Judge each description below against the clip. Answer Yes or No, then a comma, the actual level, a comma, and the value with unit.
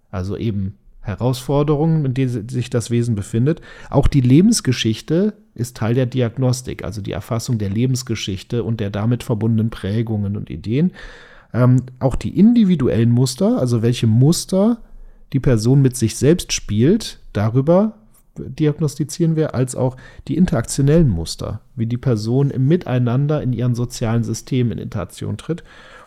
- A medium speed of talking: Yes, average, 145 wpm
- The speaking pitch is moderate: No, low, 125 Hz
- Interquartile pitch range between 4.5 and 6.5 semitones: No, average, 4.0 semitones